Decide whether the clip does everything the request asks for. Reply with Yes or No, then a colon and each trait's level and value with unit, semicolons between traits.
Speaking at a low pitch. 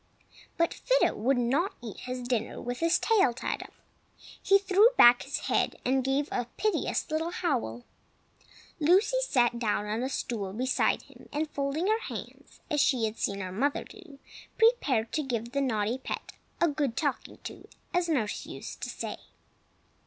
No: very high, 270 Hz